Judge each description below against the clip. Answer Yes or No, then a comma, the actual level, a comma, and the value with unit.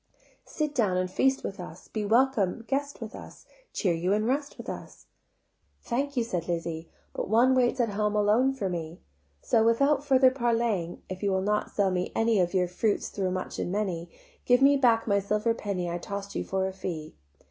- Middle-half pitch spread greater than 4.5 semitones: Yes, average, 4.9 semitones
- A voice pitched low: No, high, 210 Hz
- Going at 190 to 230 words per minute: Yes, average, 200 wpm